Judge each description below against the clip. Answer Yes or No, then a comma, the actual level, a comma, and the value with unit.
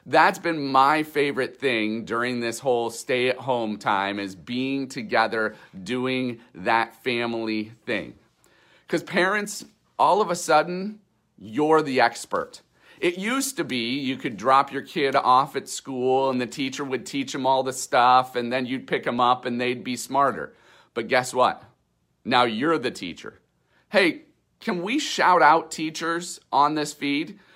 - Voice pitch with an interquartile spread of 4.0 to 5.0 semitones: Yes, average, 4.6 semitones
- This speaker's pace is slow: No, average, 165 wpm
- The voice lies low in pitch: Yes, low, 130 Hz